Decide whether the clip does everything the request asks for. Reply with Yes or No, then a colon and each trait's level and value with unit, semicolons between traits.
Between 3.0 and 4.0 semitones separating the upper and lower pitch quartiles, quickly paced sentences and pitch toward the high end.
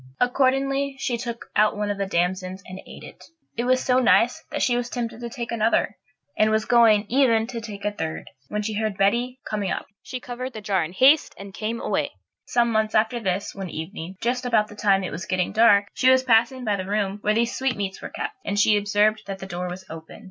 Yes: average, 3.5 semitones; fast, 230 wpm; high, 215 Hz